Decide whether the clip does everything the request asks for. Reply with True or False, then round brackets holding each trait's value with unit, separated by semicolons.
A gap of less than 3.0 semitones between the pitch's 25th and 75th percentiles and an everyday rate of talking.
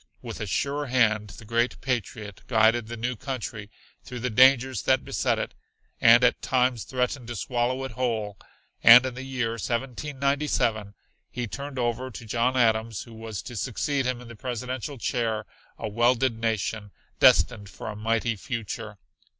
True (2.4 semitones; 165 wpm)